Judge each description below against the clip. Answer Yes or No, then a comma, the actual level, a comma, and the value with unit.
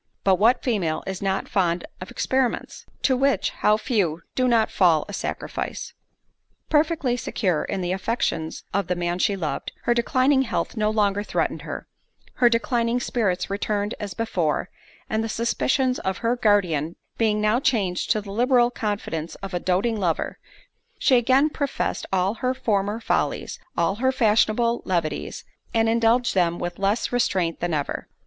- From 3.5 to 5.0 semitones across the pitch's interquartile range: Yes, average, 4.6 semitones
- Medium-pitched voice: No, high, 210 Hz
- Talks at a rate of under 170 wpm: Yes, average, 160 wpm